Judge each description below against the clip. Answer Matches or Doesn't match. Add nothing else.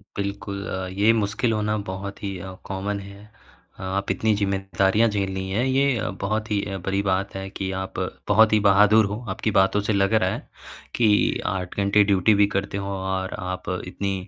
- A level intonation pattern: Matches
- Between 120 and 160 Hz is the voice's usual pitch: Doesn't match